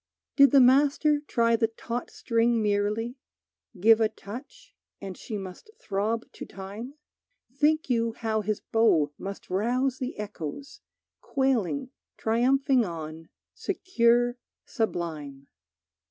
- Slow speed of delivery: Yes, slow, 115 wpm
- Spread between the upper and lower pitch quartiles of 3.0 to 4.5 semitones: Yes, average, 4.2 semitones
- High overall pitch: Yes, high, 230 Hz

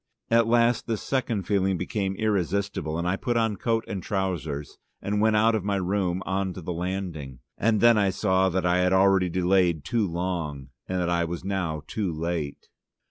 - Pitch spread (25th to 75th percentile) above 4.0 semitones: No, average, 2.9 semitones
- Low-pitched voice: Yes, very low, 95 Hz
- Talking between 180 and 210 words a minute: Yes, average, 190 wpm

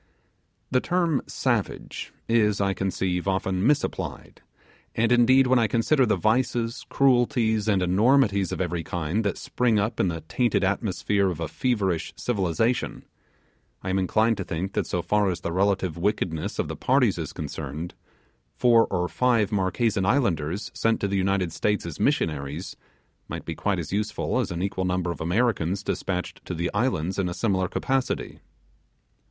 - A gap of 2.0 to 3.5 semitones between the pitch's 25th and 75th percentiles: No, average, 4.3 semitones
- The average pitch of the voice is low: Yes, low, 100 Hz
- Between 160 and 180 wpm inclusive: Yes, average, 165 wpm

